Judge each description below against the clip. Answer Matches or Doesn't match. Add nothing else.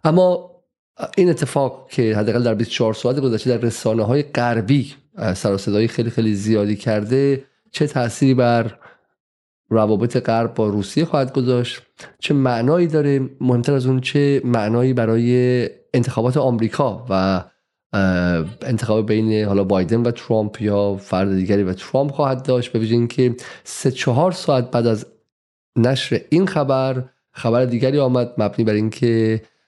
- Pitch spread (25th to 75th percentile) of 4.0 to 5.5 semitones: Doesn't match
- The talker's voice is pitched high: Doesn't match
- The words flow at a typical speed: Matches